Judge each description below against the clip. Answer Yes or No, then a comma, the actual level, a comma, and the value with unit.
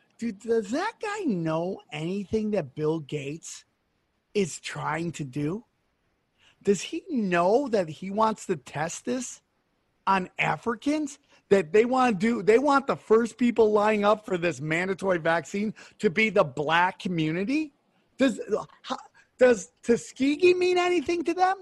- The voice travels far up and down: Yes, wide, 6.2 semitones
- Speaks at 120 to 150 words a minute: Yes, average, 145 wpm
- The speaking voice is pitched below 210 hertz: No, high, 215 Hz